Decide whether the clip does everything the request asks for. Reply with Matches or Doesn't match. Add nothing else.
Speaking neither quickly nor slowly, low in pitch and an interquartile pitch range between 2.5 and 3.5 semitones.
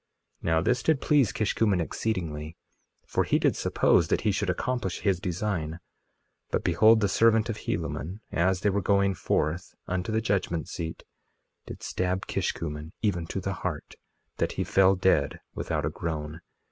Doesn't match